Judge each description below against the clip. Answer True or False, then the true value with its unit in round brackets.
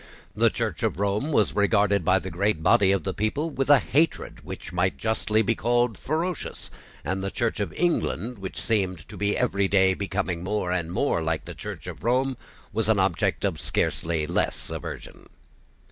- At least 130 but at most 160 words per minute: False (185 wpm)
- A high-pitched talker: False (100 Hz)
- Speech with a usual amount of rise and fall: True (3.9 semitones)